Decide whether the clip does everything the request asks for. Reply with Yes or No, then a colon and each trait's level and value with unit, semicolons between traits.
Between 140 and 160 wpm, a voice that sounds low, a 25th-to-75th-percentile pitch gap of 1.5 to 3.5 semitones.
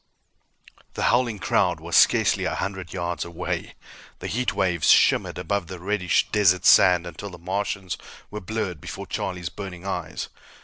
Yes: average, 150 wpm; very low, 95 Hz; narrow, 2.6 semitones